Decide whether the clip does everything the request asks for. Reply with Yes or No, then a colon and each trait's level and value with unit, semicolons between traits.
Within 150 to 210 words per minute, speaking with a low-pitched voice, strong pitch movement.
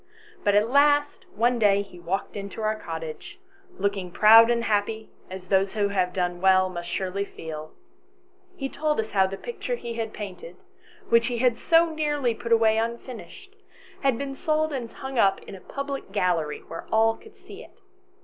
No: average, 180 wpm; high, 220 Hz; wide, 5.8 semitones